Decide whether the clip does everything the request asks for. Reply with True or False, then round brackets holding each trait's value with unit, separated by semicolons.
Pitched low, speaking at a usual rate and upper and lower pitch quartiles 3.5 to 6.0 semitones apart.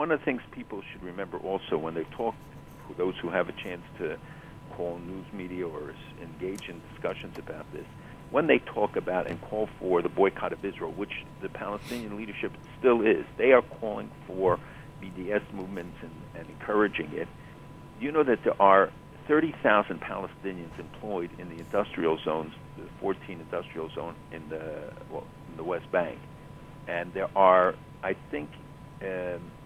True (95 Hz; 165 wpm; 5.5 semitones)